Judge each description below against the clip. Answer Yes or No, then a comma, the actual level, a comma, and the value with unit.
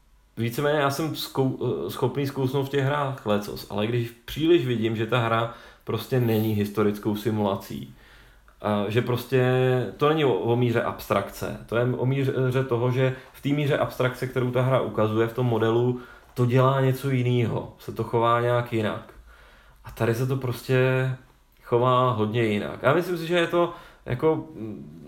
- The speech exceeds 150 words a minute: Yes, average, 165 wpm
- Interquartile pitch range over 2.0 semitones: Yes, average, 2.7 semitones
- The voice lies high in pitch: No, low, 125 Hz